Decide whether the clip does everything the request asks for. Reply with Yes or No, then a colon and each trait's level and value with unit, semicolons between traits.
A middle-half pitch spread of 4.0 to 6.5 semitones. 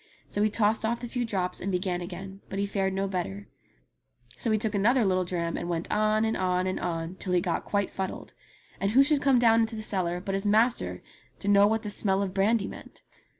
No: average, 3.0 semitones